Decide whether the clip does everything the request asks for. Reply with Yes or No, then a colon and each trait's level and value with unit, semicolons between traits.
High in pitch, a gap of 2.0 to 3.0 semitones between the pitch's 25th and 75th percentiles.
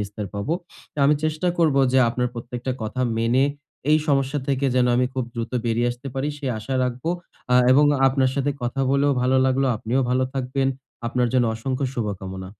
No: low, 130 Hz; narrow, 2.5 semitones